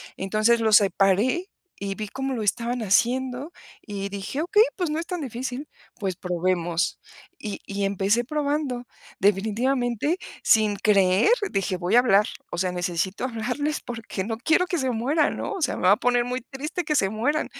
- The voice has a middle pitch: No, high, 230 Hz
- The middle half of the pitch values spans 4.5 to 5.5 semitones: Yes, average, 5.2 semitones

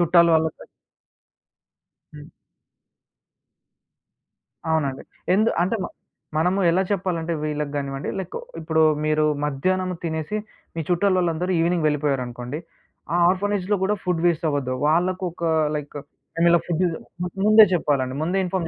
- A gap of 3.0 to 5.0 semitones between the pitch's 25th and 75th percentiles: Yes, average, 3.4 semitones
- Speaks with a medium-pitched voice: Yes, medium, 165 Hz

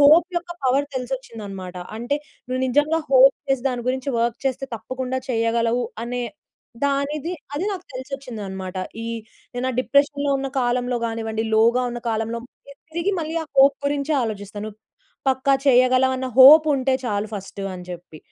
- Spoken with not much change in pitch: No, average, 3.5 semitones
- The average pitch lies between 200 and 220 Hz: No, very high, 255 Hz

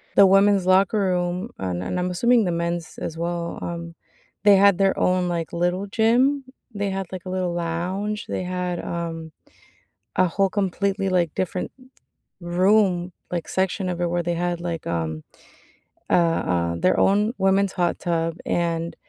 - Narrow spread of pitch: Yes, narrow, 2.3 semitones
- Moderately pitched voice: Yes, medium, 180 Hz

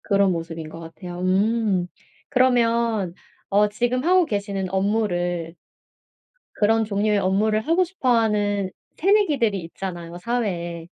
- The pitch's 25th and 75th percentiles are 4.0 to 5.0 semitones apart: Yes, average, 4.4 semitones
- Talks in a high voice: Yes, high, 205 Hz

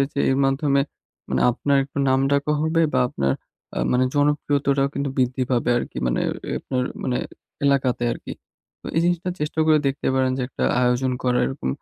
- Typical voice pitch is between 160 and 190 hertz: No, low, 135 Hz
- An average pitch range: No, narrow, 2.1 semitones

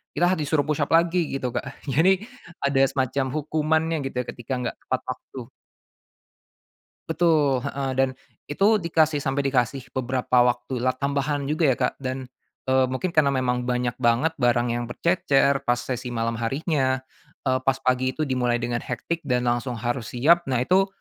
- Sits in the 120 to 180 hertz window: Yes, low, 135 Hz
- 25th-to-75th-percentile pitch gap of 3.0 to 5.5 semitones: Yes, average, 3.7 semitones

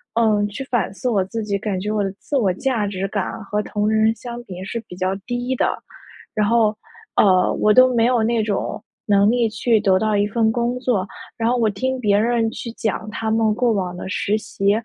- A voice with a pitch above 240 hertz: No, high, 215 Hz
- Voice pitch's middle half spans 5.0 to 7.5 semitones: No, average, 2.8 semitones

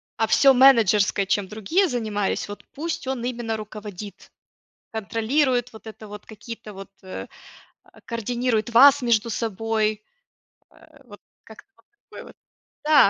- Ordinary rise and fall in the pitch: Yes, average, 3.0 semitones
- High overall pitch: Yes, high, 225 Hz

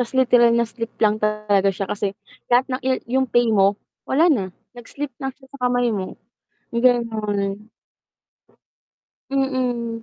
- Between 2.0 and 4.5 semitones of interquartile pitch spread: Yes, average, 3.3 semitones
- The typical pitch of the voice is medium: No, high, 235 Hz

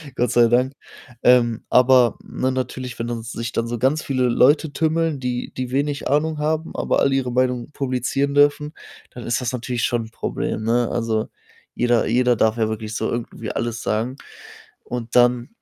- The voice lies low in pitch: Yes, low, 125 Hz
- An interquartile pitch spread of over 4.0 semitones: No, narrow, 2.4 semitones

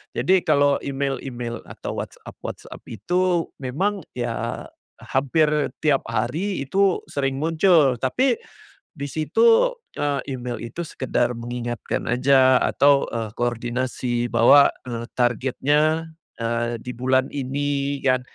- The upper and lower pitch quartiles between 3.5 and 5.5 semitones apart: Yes, average, 3.8 semitones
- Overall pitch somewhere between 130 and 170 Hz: Yes, low, 135 Hz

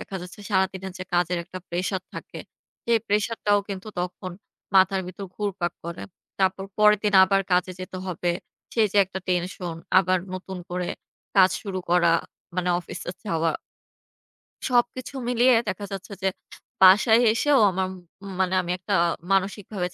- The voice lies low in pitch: No, high, 190 Hz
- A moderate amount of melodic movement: No, narrow, 2.2 semitones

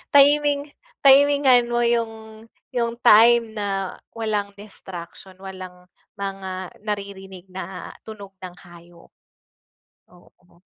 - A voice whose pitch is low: No, high, 200 Hz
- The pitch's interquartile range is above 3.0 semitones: Yes, average, 3.8 semitones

